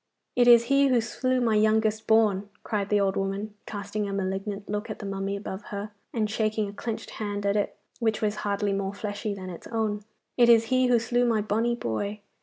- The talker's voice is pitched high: Yes, high, 210 Hz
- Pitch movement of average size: No, narrow, 2.0 semitones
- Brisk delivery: Yes, fast, 210 wpm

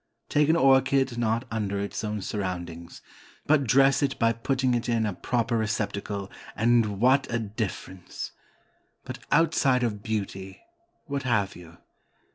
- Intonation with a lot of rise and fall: No, average, 4.6 semitones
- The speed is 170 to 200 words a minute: No, average, 140 wpm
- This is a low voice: Yes, low, 115 Hz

